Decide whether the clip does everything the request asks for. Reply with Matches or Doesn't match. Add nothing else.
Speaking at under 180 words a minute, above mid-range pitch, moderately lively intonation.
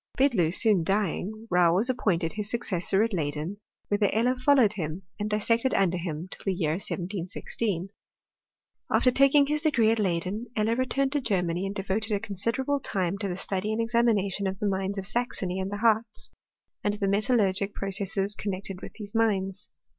Doesn't match